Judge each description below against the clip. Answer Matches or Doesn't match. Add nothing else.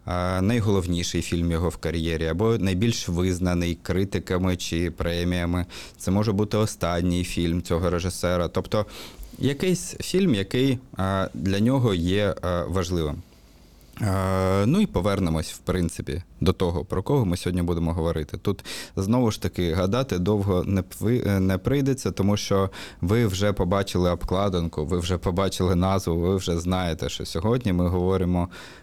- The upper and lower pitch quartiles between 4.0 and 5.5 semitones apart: Doesn't match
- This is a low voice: Matches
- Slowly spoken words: Doesn't match